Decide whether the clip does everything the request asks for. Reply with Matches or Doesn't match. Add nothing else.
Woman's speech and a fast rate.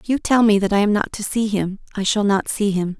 Matches